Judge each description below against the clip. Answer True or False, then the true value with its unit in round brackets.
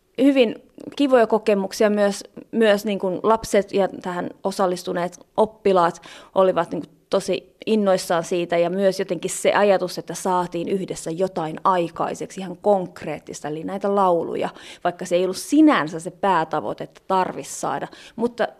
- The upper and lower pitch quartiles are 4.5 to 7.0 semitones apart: False (2.9 semitones)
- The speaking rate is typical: True (140 wpm)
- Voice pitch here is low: False (190 Hz)